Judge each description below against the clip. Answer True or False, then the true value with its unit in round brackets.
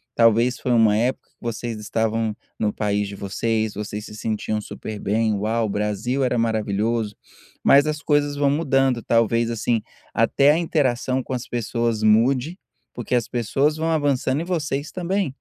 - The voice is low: True (115 Hz)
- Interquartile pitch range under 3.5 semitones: False (4.1 semitones)